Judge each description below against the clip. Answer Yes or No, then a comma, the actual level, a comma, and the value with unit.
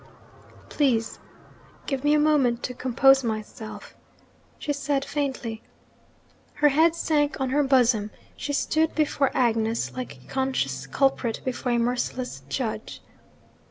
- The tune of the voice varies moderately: Yes, average, 3.6 semitones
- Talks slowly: Yes, slow, 125 wpm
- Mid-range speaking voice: No, very high, 260 Hz